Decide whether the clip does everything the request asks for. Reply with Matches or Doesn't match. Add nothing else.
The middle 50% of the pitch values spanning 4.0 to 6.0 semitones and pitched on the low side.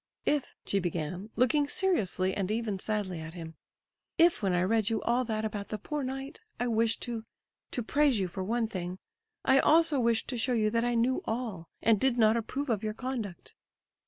Doesn't match